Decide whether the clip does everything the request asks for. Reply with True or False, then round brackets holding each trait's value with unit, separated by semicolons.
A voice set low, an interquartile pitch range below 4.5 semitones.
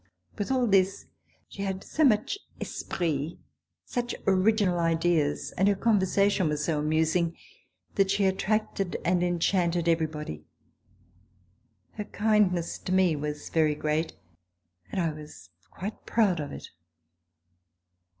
False (180 Hz; 3.9 semitones)